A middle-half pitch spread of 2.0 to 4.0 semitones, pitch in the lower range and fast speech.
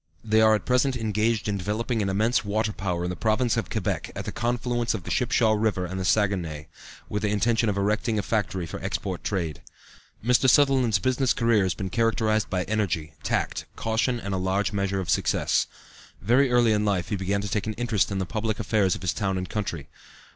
Yes: average, 3.1 semitones; low, 105 Hz; fast, 210 wpm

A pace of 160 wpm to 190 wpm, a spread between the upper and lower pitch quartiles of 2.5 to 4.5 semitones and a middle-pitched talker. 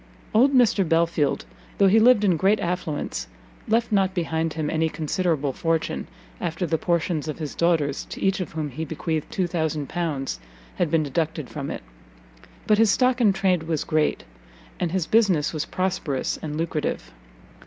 Yes: average, 165 wpm; average, 3.6 semitones; medium, 165 Hz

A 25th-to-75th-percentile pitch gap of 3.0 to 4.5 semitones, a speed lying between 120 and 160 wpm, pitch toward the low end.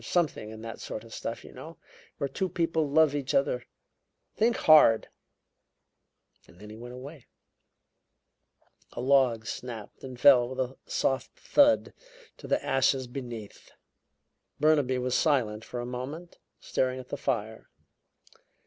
Yes: average, 4.0 semitones; average, 140 wpm; low, 130 Hz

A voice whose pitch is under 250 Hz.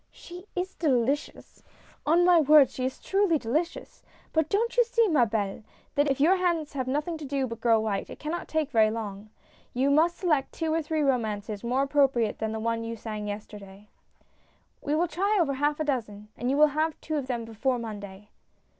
No: very high, 275 Hz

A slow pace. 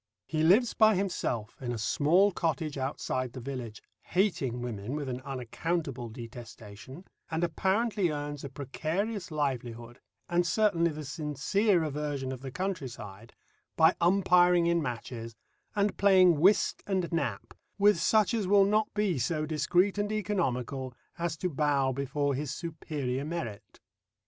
No: average, 145 wpm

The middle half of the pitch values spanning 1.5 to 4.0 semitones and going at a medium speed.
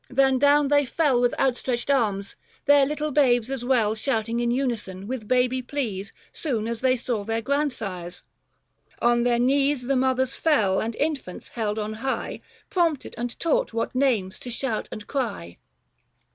Yes: average, 3.6 semitones; average, 165 wpm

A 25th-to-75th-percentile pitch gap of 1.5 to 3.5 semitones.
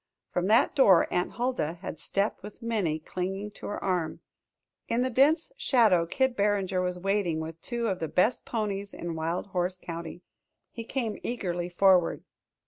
No: average, 4.4 semitones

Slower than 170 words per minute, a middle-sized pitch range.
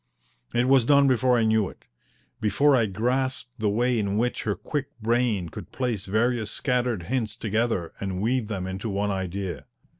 No: average, 175 wpm; average, 3.8 semitones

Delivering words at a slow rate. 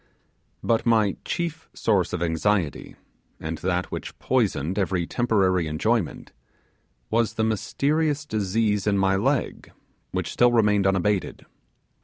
Yes: slow, 120 wpm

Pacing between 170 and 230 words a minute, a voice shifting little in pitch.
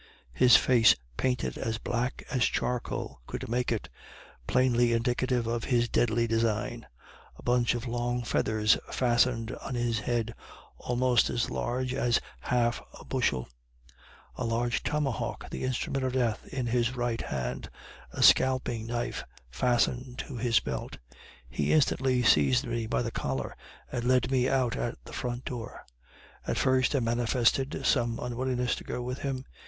No: average, 150 wpm; narrow, 1.6 semitones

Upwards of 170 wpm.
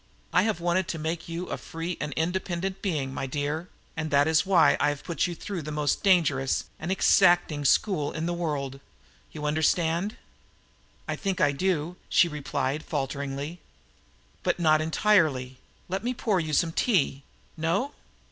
No: average, 165 wpm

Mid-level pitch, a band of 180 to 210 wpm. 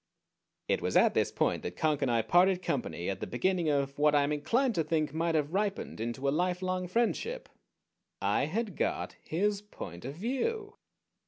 Yes: medium, 165 Hz; average, 185 wpm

